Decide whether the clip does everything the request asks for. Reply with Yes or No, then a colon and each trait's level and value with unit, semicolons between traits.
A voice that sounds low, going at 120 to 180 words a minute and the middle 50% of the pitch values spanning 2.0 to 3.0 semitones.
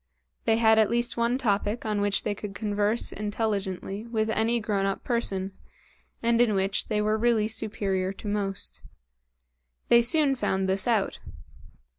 No: high, 215 Hz; average, 155 wpm; average, 2.7 semitones